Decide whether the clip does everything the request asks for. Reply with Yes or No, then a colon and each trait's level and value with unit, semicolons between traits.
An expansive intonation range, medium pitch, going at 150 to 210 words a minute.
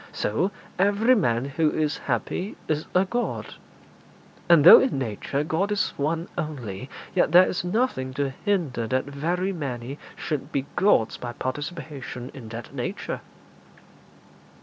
No: wide, 5.7 semitones; medium, 150 Hz; average, 140 wpm